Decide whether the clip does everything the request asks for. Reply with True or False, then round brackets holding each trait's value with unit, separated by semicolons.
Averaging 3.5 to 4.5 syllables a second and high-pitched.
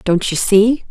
True (3.9 syllables/s; 205 Hz)